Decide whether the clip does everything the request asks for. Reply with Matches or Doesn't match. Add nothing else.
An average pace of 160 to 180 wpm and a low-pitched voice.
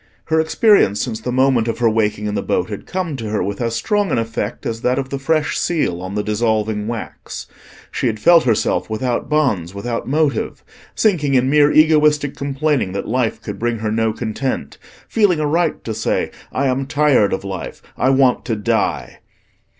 Doesn't match